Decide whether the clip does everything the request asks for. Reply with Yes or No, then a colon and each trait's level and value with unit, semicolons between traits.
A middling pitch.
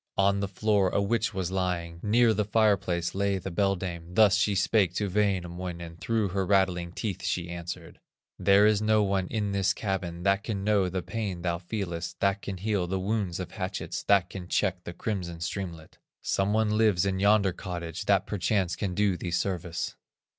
No: very low, 95 Hz